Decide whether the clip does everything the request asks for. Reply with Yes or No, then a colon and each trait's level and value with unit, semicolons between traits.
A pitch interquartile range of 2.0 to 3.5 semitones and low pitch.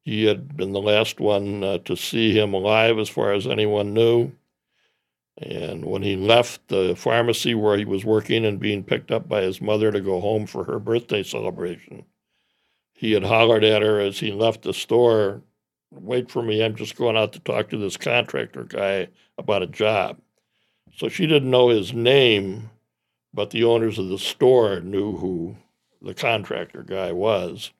Yes: narrow, 2.4 semitones; low, 105 Hz